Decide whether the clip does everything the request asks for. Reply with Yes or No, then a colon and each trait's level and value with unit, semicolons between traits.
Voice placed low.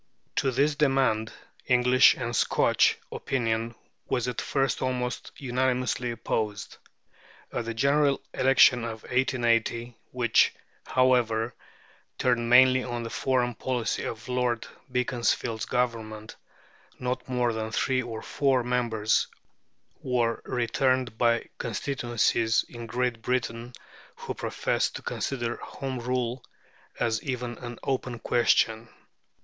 Yes: low, 120 Hz